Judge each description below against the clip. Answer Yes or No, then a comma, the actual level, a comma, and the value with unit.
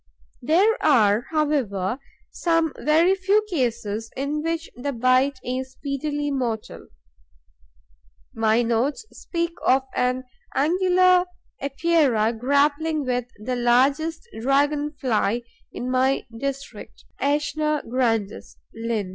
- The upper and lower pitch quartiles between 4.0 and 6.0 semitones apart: Yes, average, 4.3 semitones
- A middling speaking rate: No, slow, 105 wpm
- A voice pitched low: No, very high, 275 Hz